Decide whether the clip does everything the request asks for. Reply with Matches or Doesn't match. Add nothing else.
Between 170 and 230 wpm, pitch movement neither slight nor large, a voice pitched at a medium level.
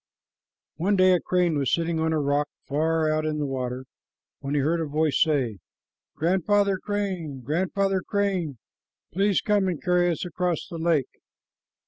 Doesn't match